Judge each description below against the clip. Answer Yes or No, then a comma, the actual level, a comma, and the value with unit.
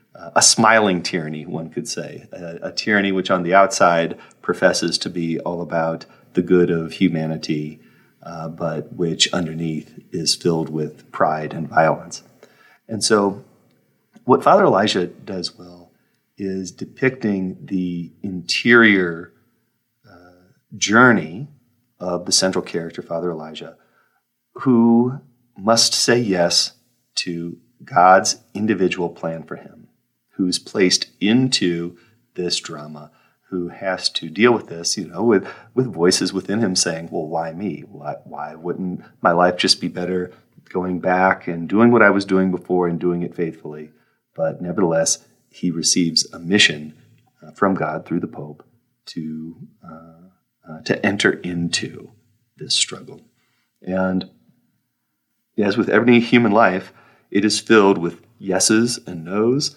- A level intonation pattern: No, average, 4.1 semitones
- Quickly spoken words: No, average, 140 wpm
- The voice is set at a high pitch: No, very low, 90 Hz